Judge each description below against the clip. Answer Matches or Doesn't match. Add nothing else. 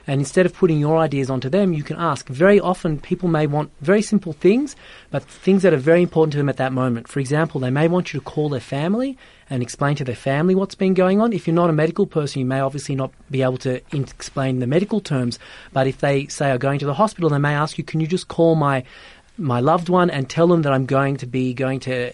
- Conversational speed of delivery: Doesn't match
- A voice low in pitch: Doesn't match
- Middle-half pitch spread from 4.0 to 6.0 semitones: Matches